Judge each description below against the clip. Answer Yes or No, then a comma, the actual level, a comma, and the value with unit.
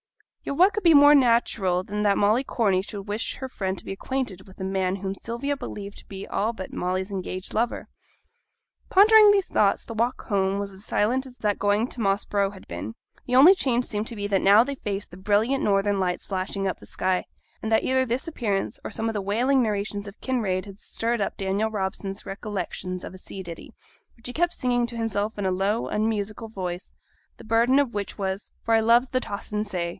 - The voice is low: No, high, 210 Hz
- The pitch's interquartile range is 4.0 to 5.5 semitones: No, average, 3.6 semitones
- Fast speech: Yes, fast, 220 wpm